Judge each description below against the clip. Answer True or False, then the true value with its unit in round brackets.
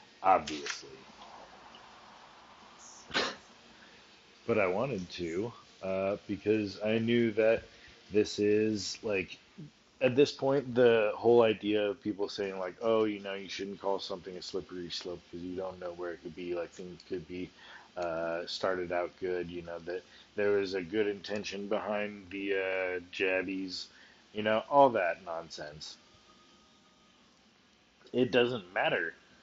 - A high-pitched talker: False (100 Hz)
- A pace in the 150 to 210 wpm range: False (140 wpm)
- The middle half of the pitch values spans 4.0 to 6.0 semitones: False (3.0 semitones)